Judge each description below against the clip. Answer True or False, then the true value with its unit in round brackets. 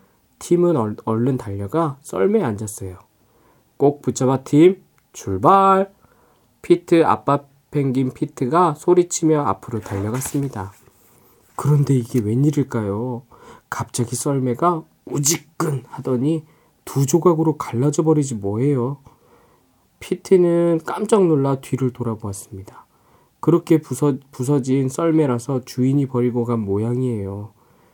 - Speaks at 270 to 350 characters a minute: False (260 characters per minute)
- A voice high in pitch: False (135 Hz)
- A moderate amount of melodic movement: True (4.9 semitones)